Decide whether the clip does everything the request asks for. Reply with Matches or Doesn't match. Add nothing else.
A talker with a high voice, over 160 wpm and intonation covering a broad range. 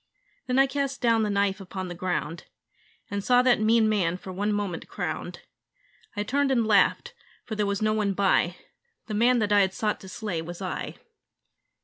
Doesn't match